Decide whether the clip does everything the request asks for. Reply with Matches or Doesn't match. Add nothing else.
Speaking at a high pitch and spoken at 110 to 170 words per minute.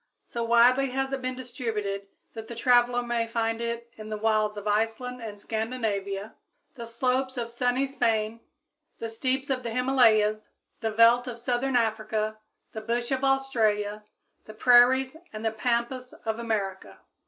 Matches